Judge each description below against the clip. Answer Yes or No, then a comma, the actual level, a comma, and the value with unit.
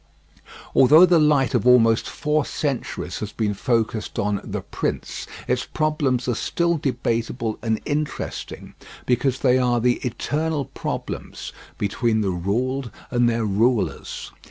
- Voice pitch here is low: Yes, low, 125 Hz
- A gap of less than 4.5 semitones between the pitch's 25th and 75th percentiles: Yes, average, 3.7 semitones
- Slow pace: Yes, slow, 130 wpm